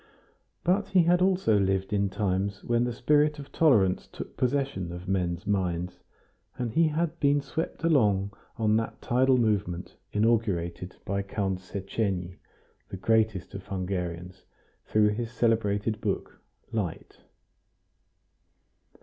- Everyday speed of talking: No, slow, 125 wpm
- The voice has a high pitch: No, low, 105 Hz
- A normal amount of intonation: Yes, average, 4.5 semitones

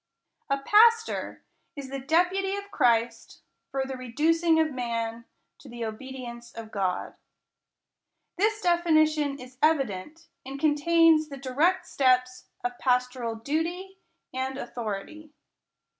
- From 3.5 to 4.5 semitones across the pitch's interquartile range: No, average, 4.9 semitones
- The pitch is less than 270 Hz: No, very high, 275 Hz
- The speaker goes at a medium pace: No, slow, 125 wpm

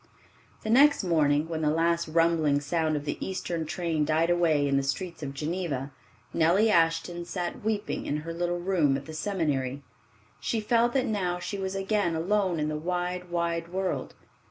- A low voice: No, medium, 170 Hz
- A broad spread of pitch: No, average, 3.2 semitones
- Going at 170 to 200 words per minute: Yes, average, 180 wpm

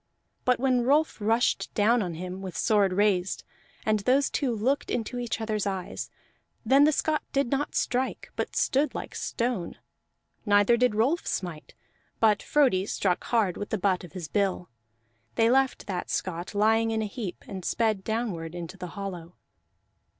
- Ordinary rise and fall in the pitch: Yes, average, 4.6 semitones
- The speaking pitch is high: Yes, high, 215 Hz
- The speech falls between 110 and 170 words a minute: Yes, average, 165 wpm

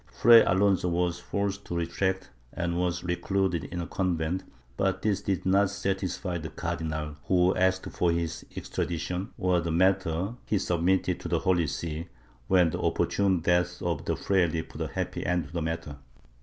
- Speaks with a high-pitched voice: No, very low, 90 Hz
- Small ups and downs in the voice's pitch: Yes, narrow, 2.1 semitones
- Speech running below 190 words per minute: Yes, average, 175 wpm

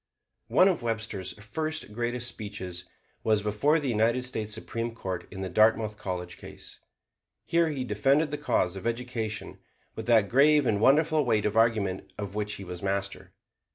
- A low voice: Yes, low, 110 Hz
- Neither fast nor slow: Yes, average, 165 wpm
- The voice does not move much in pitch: No, average, 3.8 semitones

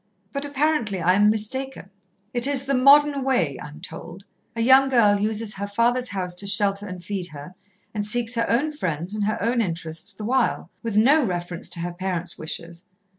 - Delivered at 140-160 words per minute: No, average, 195 wpm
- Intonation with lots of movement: Yes, wide, 5.7 semitones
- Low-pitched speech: No, high, 210 Hz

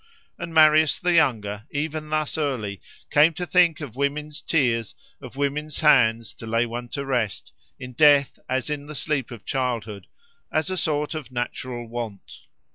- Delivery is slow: No, average, 165 wpm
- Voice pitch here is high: No, medium, 140 Hz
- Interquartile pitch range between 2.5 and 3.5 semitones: No, average, 4.3 semitones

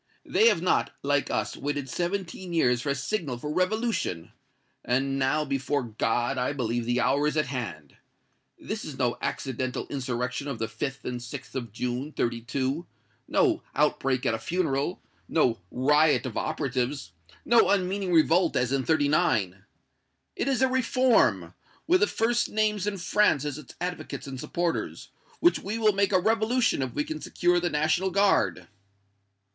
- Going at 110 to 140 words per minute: No, average, 160 wpm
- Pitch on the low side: No, medium, 145 Hz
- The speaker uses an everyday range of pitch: No, wide, 6.7 semitones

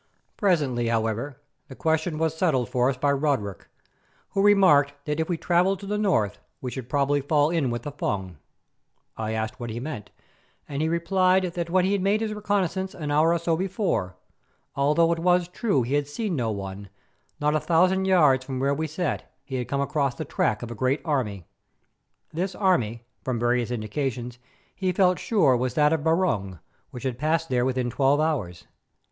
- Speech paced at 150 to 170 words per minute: No, average, 190 wpm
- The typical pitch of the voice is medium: Yes, medium, 145 Hz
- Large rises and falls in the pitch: Yes, wide, 5.9 semitones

